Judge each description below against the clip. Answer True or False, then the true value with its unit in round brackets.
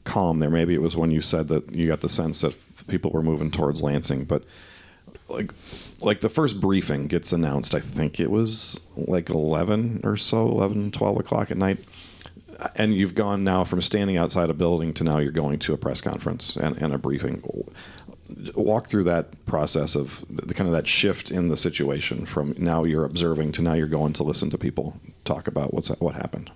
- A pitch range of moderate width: True (4.1 semitones)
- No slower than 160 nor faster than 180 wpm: False (205 wpm)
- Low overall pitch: True (85 Hz)